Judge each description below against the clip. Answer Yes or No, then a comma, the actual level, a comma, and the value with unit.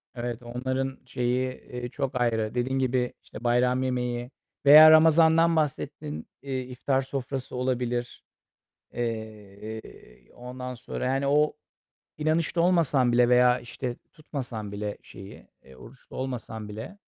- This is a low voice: Yes, low, 125 Hz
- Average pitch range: No, narrow, 2.1 semitones